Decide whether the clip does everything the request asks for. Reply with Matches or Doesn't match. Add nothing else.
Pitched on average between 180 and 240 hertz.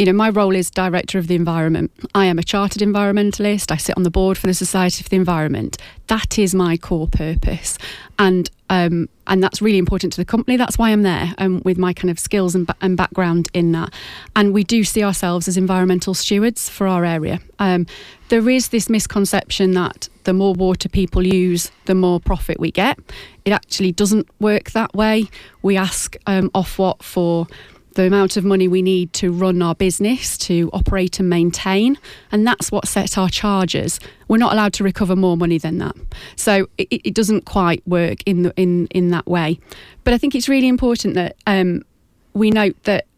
Matches